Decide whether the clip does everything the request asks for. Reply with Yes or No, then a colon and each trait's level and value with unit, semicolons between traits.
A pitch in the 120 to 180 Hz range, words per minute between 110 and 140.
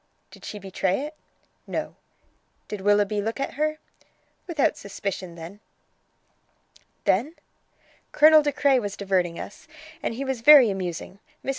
No: high, 210 Hz; slow, 135 wpm